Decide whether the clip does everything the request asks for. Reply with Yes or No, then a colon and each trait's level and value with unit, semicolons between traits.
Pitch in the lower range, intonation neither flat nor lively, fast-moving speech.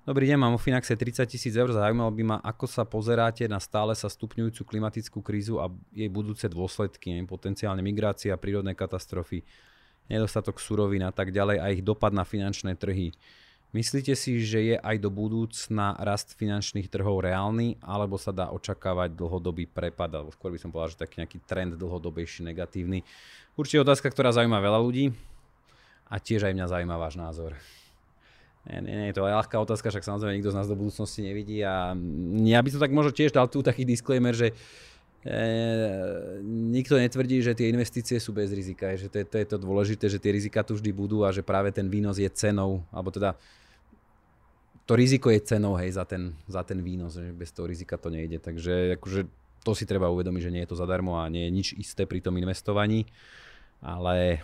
Yes: low, 100 Hz; average, 3.4 semitones; fast, 195 wpm